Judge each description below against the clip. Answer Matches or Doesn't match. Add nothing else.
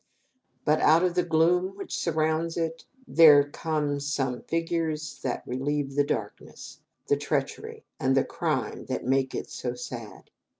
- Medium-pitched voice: Matches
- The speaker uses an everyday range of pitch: Matches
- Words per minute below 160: Matches